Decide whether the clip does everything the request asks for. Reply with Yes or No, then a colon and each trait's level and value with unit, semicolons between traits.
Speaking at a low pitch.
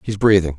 Yes: very low, 95 Hz